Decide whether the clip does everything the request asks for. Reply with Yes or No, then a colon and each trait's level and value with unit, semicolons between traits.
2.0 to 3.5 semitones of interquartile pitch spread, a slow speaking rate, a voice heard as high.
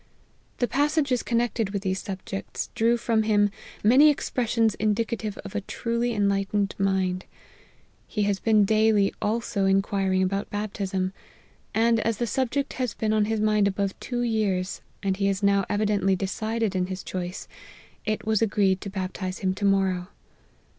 No: narrow, 2.5 semitones; average, 160 wpm; high, 205 Hz